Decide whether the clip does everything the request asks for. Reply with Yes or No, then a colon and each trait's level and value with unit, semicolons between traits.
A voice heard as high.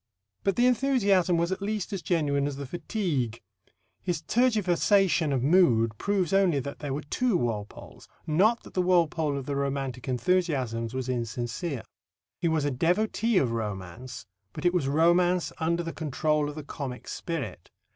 No: medium, 155 Hz